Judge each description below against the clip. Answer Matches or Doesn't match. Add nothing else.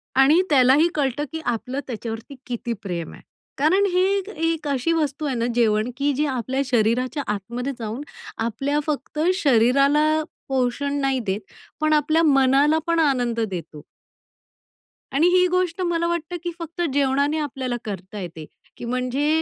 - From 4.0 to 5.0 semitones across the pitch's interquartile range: Matches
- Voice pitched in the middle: Doesn't match